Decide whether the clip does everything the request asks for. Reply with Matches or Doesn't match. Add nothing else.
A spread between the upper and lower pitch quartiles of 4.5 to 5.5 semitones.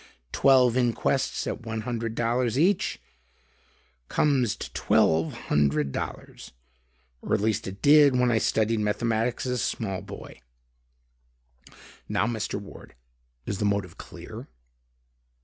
Doesn't match